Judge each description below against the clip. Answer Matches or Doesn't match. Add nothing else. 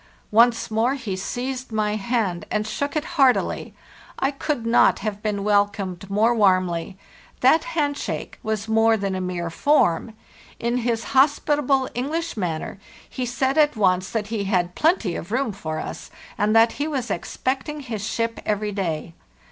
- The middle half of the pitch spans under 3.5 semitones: Doesn't match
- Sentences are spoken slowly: Doesn't match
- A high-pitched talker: Matches